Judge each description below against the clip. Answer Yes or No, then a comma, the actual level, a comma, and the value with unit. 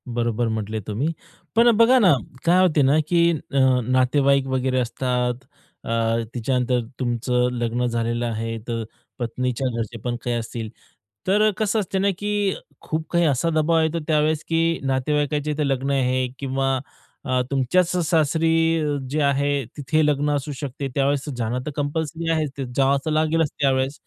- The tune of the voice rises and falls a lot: No, average, 4.1 semitones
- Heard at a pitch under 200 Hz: Yes, medium, 140 Hz